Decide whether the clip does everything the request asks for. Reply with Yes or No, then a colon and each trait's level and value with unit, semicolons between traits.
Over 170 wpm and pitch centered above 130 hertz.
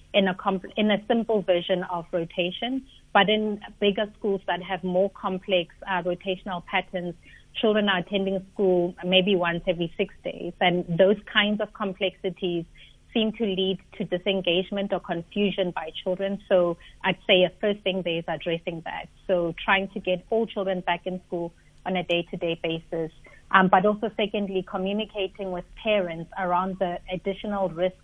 No: average, 165 wpm; high, 190 Hz